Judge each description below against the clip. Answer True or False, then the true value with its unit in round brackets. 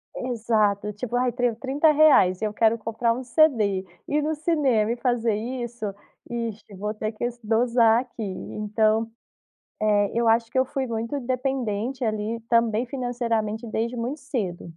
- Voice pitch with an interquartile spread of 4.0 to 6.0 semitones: False (2.7 semitones)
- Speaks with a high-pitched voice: True (230 Hz)